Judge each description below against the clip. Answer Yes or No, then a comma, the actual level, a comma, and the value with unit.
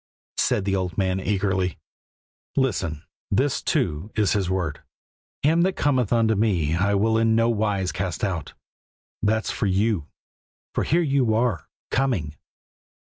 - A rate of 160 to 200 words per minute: No, average, 145 wpm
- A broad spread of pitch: No, average, 3.5 semitones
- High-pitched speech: No, low, 100 Hz